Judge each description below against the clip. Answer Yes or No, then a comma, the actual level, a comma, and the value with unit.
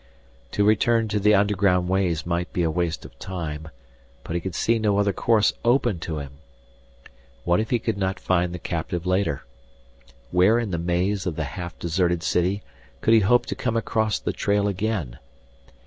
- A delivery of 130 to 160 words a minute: No, average, 185 wpm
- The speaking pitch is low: Yes, very low, 95 Hz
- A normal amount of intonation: Yes, average, 3.4 semitones